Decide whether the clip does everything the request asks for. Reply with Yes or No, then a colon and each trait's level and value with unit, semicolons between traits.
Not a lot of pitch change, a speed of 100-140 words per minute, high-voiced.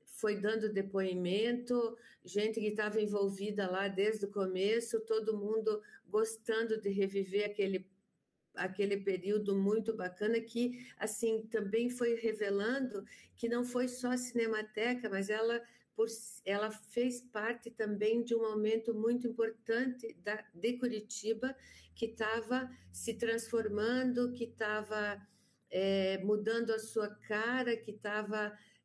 Yes: narrow, 1.9 semitones; average, 125 wpm; high, 220 Hz